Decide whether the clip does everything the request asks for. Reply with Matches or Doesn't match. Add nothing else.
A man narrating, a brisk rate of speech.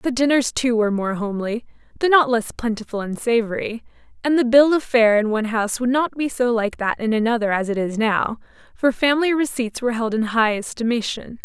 Doesn't match